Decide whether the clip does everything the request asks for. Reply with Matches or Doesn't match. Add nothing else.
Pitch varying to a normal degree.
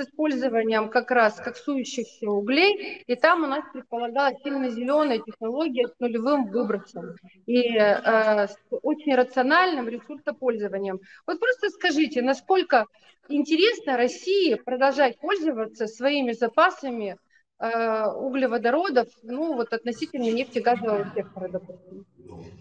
Matches